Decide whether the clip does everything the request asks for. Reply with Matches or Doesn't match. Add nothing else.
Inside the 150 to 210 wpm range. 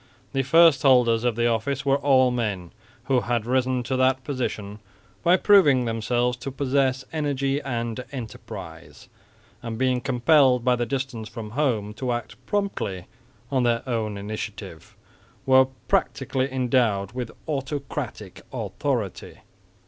Doesn't match